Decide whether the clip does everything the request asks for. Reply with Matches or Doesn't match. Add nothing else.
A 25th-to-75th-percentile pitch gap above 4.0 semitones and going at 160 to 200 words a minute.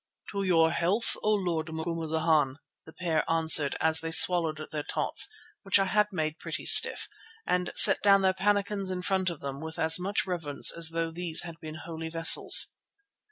Doesn't match